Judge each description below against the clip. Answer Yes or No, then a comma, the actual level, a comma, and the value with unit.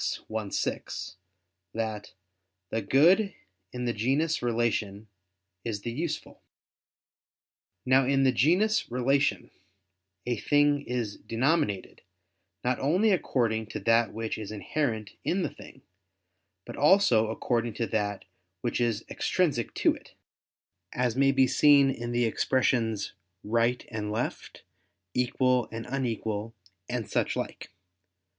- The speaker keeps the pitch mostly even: No, average, 3.6 semitones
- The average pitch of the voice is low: Yes, low, 120 Hz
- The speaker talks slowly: Yes, slow, 125 wpm